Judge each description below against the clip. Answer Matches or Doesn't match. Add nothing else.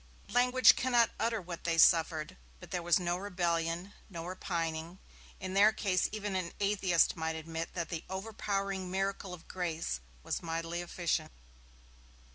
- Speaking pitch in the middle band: Matches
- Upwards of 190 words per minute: Doesn't match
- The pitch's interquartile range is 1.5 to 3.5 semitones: Matches